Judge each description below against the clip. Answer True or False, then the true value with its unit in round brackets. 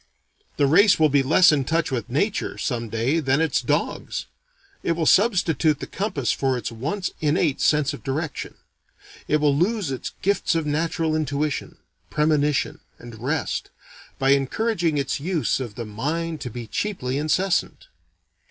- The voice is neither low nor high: True (150 Hz)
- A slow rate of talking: False (155 wpm)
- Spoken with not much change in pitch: False (3.7 semitones)